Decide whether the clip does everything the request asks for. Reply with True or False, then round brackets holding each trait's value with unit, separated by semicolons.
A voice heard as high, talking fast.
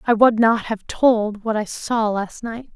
True (220 Hz; 220 wpm)